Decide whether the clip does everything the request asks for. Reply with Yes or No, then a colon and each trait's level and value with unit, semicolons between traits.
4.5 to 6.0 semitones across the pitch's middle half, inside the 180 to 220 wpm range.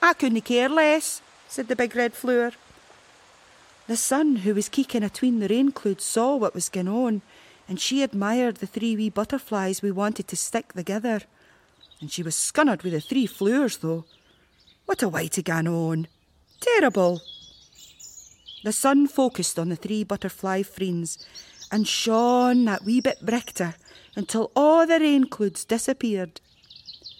No: average, 4.8 semitones; average, 155 wpm